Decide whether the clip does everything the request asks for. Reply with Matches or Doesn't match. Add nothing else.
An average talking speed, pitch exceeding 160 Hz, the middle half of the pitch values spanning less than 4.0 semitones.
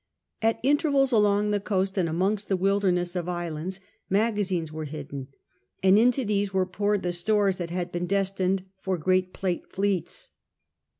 Matches